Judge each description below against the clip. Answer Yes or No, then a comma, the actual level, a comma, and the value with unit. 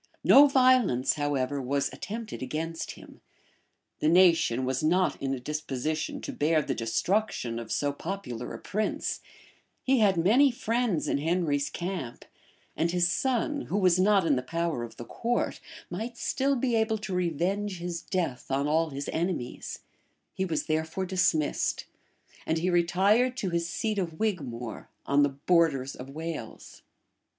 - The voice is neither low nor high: Yes, medium, 170 Hz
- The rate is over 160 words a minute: No, average, 155 wpm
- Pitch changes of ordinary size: No, wide, 5.8 semitones